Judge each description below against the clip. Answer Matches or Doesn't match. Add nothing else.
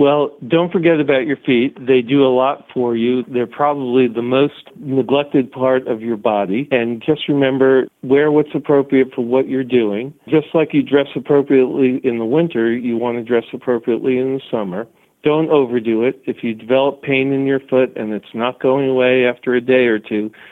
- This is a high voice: Doesn't match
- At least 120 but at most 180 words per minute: Doesn't match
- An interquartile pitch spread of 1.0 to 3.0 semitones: Matches